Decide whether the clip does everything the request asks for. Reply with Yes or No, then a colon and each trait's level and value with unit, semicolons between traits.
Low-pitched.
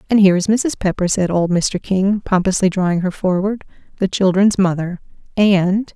No: high, 190 Hz